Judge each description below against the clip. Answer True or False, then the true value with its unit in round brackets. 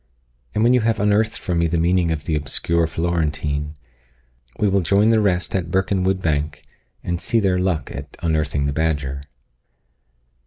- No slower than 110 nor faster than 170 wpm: True (165 wpm)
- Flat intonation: False (3.9 semitones)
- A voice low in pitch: True (85 Hz)